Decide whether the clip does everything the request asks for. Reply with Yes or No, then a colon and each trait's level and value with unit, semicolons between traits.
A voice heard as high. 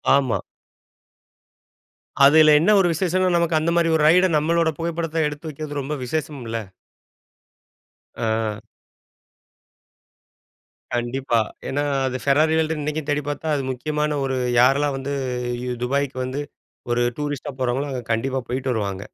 No: medium, 145 Hz